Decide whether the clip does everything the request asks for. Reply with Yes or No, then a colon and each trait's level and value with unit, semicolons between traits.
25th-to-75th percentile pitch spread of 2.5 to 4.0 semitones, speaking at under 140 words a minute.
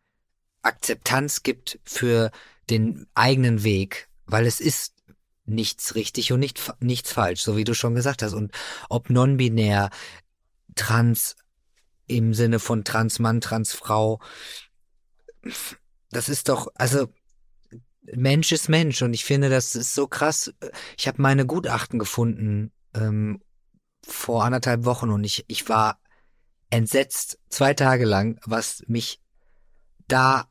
Yes: average, 2.9 semitones; average, 130 wpm